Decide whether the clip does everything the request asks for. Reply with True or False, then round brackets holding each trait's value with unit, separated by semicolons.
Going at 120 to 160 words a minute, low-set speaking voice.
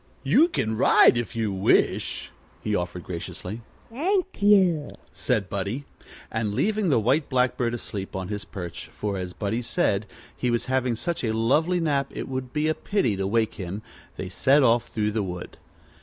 False (175 wpm; 115 Hz)